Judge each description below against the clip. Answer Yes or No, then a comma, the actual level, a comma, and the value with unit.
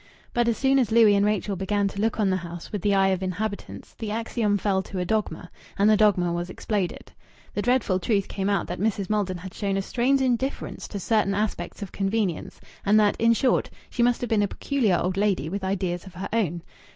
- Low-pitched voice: No, high, 200 Hz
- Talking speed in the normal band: No, fast, 225 wpm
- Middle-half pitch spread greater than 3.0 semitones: No, average, 2.7 semitones